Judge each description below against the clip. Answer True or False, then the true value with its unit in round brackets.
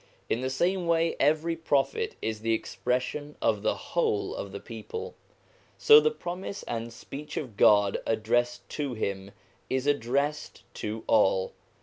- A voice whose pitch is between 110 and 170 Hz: True (140 Hz)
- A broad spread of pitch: True (7.2 semitones)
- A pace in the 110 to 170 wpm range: True (145 wpm)